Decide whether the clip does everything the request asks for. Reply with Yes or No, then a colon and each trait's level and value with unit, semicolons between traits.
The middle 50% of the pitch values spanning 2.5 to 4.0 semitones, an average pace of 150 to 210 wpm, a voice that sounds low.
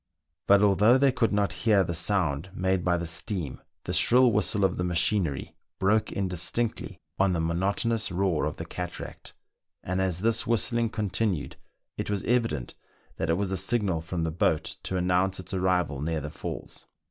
Yes: average, 3.7 semitones; average, 180 wpm; very low, 95 Hz